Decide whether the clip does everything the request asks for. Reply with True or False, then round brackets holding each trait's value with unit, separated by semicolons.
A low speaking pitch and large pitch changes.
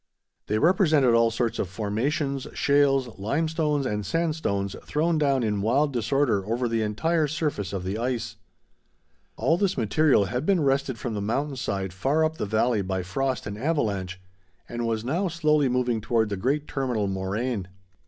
True (125 Hz; 5.9 semitones)